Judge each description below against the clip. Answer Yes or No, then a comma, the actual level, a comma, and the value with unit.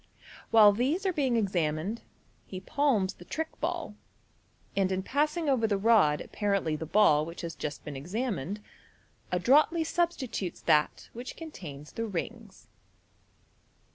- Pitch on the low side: No, high, 210 Hz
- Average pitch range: No, wide, 7.7 semitones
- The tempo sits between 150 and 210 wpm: No, average, 140 wpm